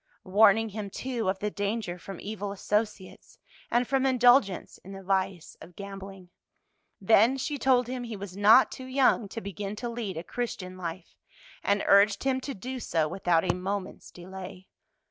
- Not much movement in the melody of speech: No, average, 3.9 semitones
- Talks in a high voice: Yes, high, 200 Hz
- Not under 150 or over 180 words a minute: Yes, average, 170 wpm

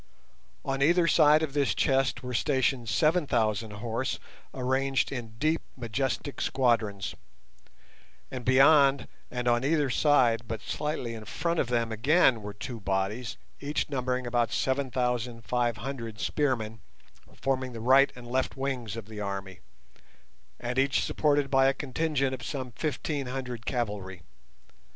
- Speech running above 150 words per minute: No, average, 145 wpm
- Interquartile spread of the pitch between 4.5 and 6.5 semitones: No, average, 3.0 semitones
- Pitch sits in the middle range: No, low, 125 Hz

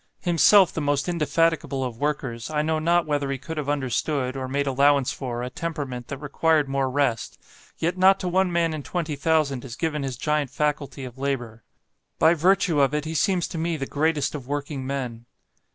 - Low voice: No, medium, 145 Hz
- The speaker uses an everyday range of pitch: Yes, average, 3.3 semitones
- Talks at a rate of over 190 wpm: Yes, average, 200 wpm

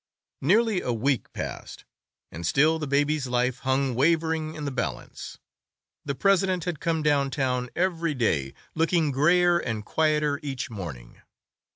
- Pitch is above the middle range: No, medium, 145 Hz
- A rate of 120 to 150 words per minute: Yes, average, 145 wpm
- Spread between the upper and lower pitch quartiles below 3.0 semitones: No, average, 4.3 semitones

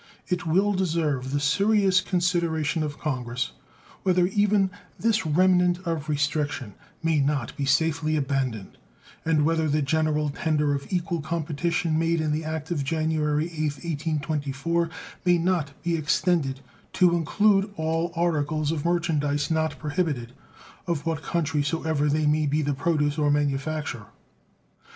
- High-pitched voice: No, medium, 155 Hz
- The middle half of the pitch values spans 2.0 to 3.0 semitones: Yes, narrow, 2.6 semitones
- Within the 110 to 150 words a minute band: Yes, average, 140 wpm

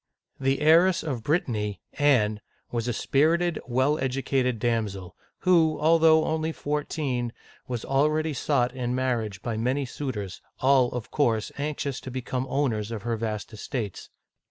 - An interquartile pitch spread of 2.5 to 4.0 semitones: No, average, 4.4 semitones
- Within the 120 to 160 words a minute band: Yes, average, 155 wpm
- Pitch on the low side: Yes, low, 130 Hz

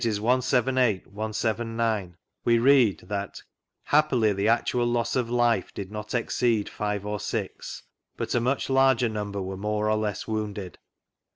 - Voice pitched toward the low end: Yes, low, 110 Hz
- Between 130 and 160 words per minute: Yes, average, 145 wpm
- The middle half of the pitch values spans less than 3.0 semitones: Yes, narrow, 2.6 semitones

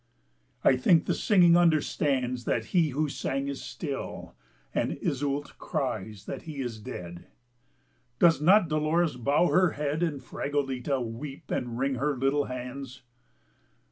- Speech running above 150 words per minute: No, average, 140 wpm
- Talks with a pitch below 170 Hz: Yes, medium, 140 Hz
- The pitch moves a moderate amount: Yes, average, 3.3 semitones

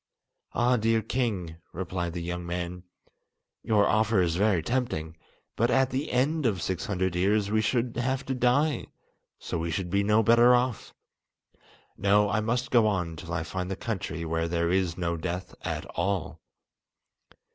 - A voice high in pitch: No, low, 100 Hz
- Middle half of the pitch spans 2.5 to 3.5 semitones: No, average, 5.2 semitones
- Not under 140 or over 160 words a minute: No, average, 170 wpm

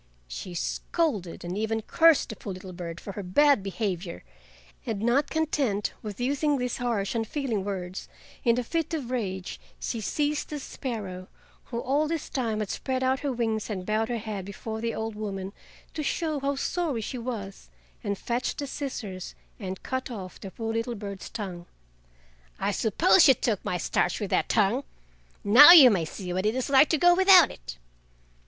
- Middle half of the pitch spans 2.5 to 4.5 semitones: No, wide, 5.5 semitones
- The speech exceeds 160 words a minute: Yes, average, 180 wpm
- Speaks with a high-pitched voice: Yes, high, 225 Hz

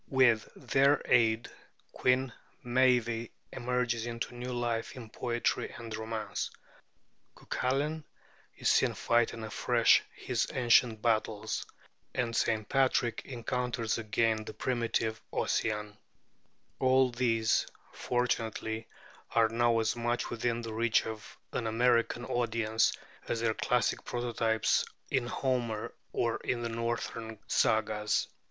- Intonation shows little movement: Yes, narrow, 1.7 semitones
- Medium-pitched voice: No, low, 115 Hz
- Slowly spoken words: Yes, slow, 115 wpm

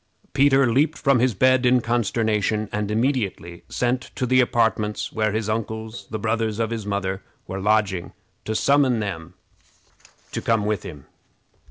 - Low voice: Yes, low, 110 Hz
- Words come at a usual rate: Yes, average, 155 wpm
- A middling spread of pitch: Yes, average, 3.1 semitones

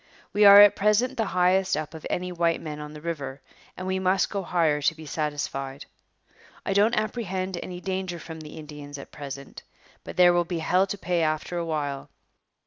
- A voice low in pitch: No, medium, 175 Hz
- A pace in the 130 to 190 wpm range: No, average, 200 wpm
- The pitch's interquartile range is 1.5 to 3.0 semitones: No, average, 3.8 semitones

